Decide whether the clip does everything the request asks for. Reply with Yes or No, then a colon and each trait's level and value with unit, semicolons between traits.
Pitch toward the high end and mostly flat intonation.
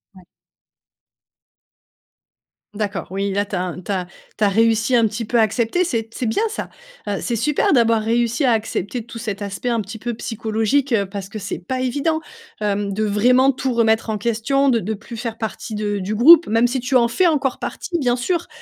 No: high, 225 Hz; average, 3.2 semitones